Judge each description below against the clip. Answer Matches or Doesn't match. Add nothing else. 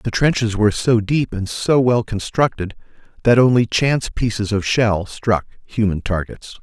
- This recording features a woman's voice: Doesn't match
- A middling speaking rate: Matches